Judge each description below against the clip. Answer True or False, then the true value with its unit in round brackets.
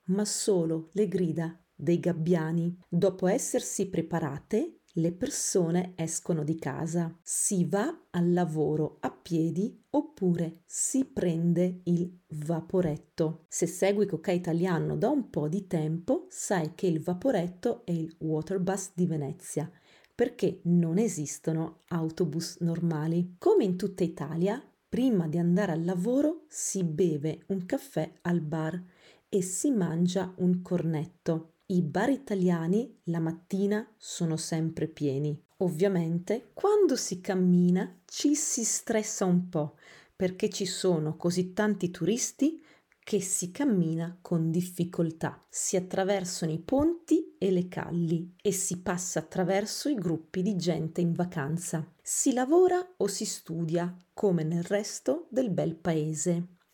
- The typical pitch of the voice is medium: True (180 Hz)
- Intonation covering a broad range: False (3.5 semitones)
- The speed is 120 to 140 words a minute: True (130 wpm)